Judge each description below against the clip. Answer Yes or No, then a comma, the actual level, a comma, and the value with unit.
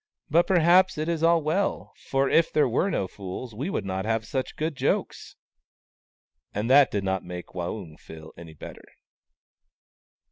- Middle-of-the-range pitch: No, low, 120 Hz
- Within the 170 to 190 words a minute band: Yes, average, 175 wpm